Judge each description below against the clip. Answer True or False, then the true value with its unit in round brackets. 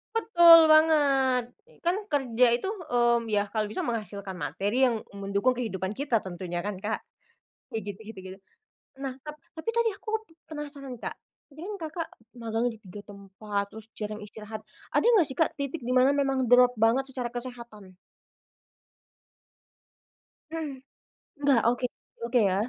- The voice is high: True (245 Hz)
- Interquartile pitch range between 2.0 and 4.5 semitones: False (5.3 semitones)